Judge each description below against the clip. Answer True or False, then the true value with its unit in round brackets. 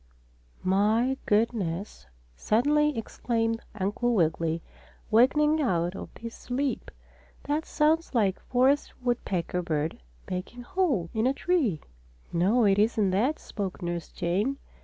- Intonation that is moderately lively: False (6.1 semitones)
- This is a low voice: False (225 Hz)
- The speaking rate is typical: False (120 wpm)